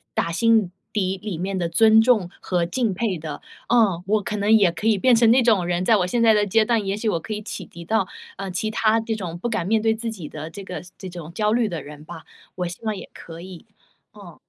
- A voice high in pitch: Yes, high, 200 Hz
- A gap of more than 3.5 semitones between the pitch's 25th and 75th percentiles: Yes, average, 4.1 semitones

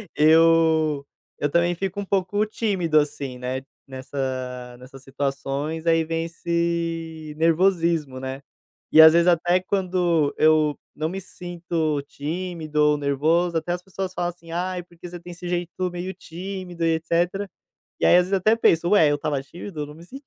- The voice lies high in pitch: No, medium, 165 Hz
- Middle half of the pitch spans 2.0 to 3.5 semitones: Yes, average, 3.0 semitones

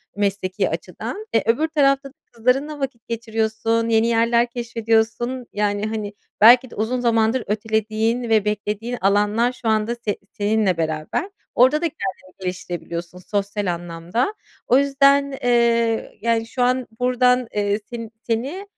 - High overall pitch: Yes, high, 230 Hz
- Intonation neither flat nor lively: Yes, average, 3.1 semitones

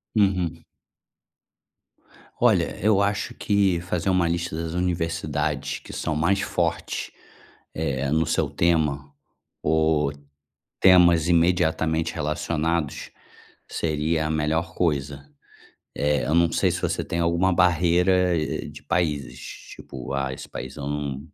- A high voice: No, very low, 80 Hz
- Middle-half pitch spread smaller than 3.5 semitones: Yes, average, 2.9 semitones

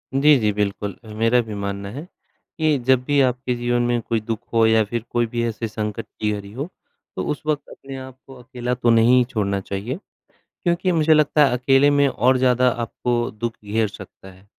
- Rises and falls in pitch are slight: No, average, 3.6 semitones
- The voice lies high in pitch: No, low, 120 Hz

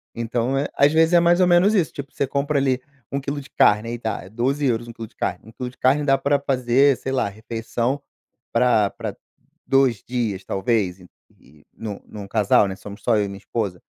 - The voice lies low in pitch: Yes, low, 120 Hz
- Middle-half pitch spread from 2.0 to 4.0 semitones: No, average, 4.6 semitones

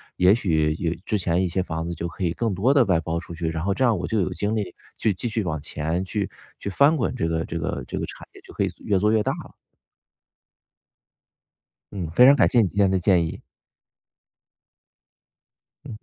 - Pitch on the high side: No, very low, 95 Hz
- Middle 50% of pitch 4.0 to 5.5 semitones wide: Yes, average, 4.4 semitones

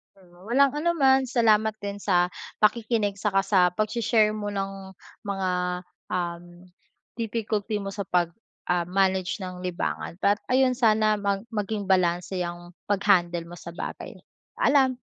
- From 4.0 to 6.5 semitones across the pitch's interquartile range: No, average, 3.1 semitones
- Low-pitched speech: No, high, 200 Hz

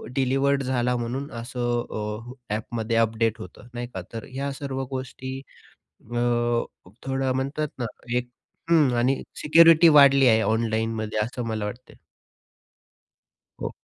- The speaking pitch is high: No, low, 120 Hz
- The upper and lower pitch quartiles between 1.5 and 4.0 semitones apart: Yes, average, 2.9 semitones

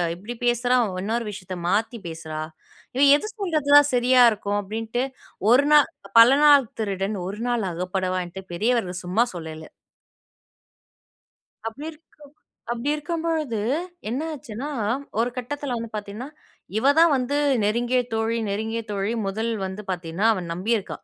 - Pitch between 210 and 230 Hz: Yes, high, 225 Hz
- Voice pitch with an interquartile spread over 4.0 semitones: Yes, average, 4.5 semitones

